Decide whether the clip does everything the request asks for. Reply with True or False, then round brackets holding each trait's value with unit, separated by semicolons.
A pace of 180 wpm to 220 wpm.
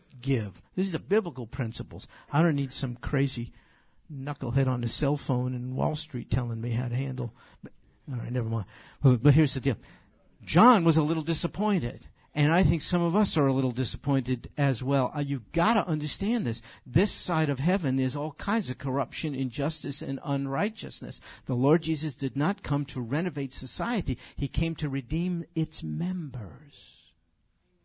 True (185 wpm)